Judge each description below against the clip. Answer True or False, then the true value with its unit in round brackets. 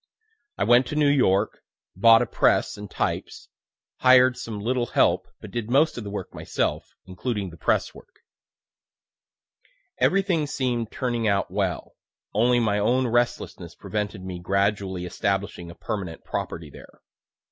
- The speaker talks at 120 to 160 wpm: True (145 wpm)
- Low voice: True (110 Hz)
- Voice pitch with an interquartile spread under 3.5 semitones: False (4.2 semitones)